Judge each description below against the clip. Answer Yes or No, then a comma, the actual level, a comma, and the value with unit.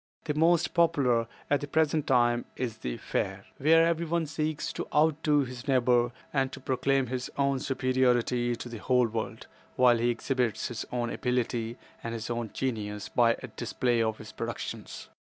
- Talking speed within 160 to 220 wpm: Yes, average, 170 wpm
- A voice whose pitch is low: Yes, low, 125 Hz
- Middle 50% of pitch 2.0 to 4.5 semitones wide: Yes, average, 3.4 semitones